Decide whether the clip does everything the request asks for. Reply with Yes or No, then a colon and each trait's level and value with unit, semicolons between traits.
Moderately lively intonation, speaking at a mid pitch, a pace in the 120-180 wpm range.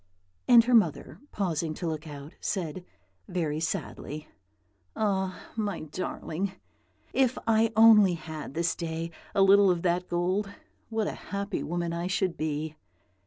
Yes: average, 3.9 semitones; medium, 180 Hz; average, 140 wpm